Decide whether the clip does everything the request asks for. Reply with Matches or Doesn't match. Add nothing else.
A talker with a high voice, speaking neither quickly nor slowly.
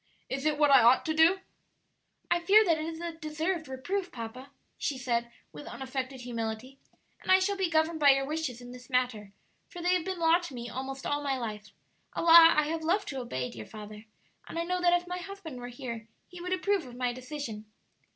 Doesn't match